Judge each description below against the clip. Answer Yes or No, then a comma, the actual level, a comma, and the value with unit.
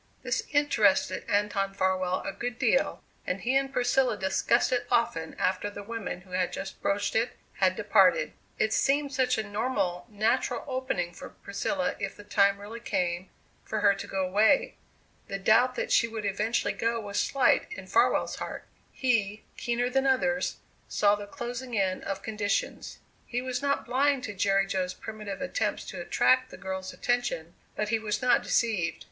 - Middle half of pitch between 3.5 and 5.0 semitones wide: Yes, average, 4.2 semitones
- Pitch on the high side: Yes, high, 215 Hz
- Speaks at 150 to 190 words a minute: Yes, average, 175 wpm